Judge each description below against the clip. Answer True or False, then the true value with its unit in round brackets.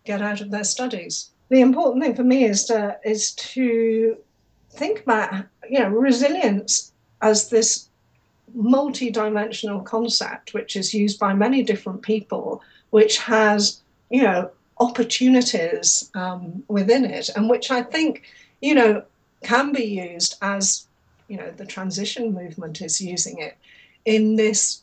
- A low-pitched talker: False (220 Hz)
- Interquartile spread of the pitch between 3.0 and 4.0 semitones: True (3.3 semitones)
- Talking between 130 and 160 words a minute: True (145 wpm)